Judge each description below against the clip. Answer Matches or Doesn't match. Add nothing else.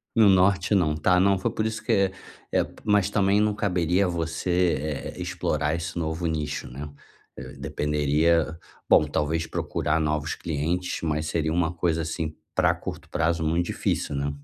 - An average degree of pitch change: Matches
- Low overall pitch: Matches